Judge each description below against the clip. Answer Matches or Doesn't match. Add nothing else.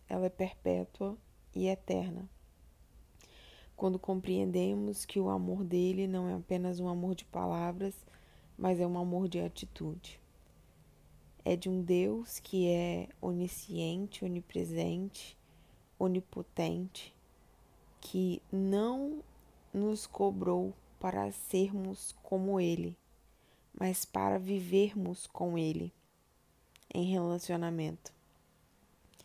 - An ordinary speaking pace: Doesn't match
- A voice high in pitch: Doesn't match